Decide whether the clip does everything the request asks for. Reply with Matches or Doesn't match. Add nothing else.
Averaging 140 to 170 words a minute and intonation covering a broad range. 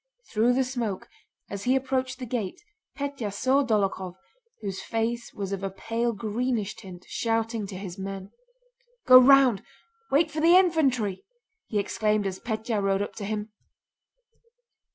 Doesn't match